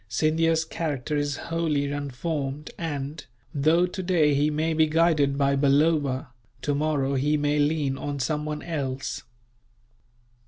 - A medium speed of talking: No, slow, 120 wpm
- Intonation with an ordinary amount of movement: No, narrow, 2.2 semitones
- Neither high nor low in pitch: Yes, medium, 150 Hz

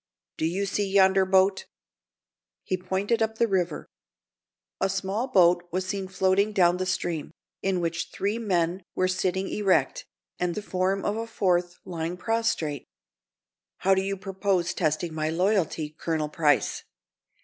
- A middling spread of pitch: No, narrow, 2.2 semitones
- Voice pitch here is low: No, medium, 185 Hz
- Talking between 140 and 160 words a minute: Yes, average, 150 wpm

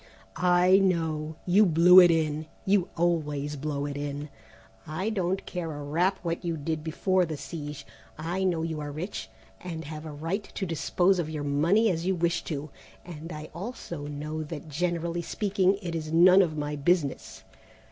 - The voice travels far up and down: No, average, 2.9 semitones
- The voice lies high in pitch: No, medium, 165 Hz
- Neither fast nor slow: Yes, average, 180 wpm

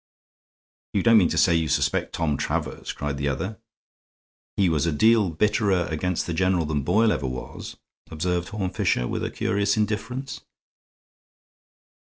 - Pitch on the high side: No, very low, 90 Hz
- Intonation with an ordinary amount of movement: Yes, average, 5.0 semitones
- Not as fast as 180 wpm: Yes, average, 155 wpm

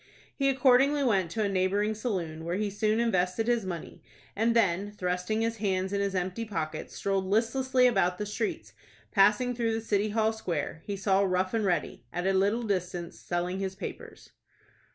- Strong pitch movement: No, average, 3.5 semitones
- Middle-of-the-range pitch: No, high, 200 Hz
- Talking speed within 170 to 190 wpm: Yes, average, 180 wpm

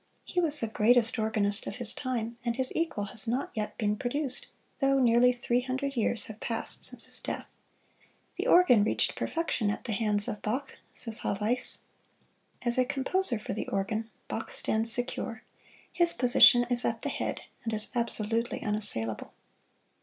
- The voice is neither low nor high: No, high, 235 Hz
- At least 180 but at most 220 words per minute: No, average, 170 wpm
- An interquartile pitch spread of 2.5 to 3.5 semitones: Yes, average, 2.9 semitones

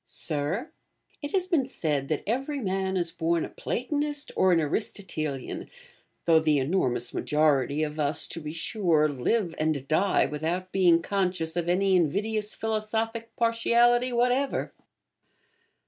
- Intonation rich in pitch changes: Yes, wide, 6.6 semitones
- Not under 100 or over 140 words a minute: Yes, slow, 135 wpm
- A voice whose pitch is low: No, medium, 180 Hz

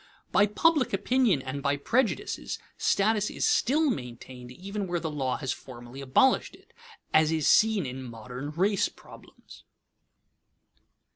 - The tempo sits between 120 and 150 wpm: Yes, slow, 135 wpm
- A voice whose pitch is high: No, medium, 160 Hz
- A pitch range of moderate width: No, wide, 8.3 semitones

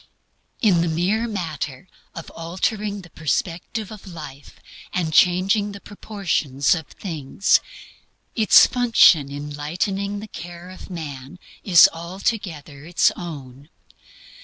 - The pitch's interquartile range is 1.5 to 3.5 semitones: No, average, 4.7 semitones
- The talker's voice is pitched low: No, medium, 175 Hz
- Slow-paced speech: Yes, slow, 115 wpm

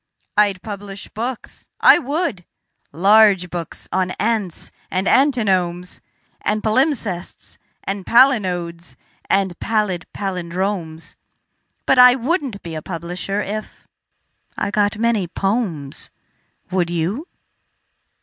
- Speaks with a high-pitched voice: Yes, high, 200 Hz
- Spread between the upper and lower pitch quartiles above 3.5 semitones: Yes, average, 3.9 semitones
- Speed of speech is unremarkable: No, slow, 100 wpm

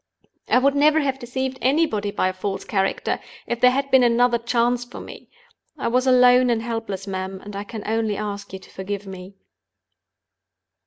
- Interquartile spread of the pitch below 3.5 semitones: No, average, 4.0 semitones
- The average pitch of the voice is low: No, high, 235 Hz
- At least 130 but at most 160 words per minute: No, average, 180 wpm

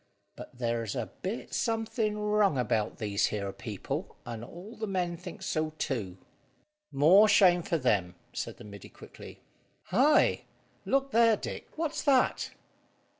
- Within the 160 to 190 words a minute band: No, average, 140 wpm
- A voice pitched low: No, medium, 175 Hz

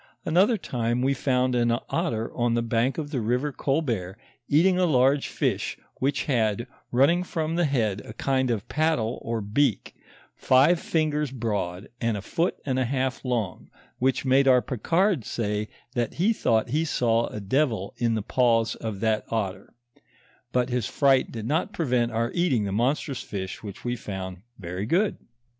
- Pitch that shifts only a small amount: No, average, 4.4 semitones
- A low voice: Yes, low, 125 Hz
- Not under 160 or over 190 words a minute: Yes, average, 175 wpm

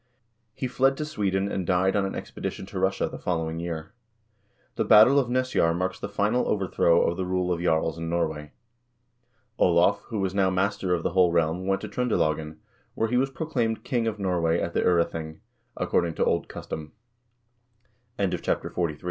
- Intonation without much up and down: No, average, 4.2 semitones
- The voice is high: No, very low, 95 Hz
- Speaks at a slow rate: No, average, 175 wpm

